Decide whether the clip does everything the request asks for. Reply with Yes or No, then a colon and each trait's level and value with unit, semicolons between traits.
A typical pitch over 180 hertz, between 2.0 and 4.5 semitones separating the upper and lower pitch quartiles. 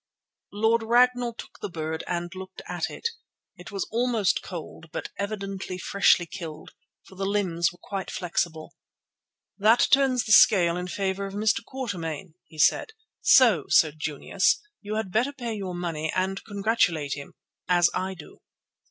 Yes: high, 190 Hz; average, 4.1 semitones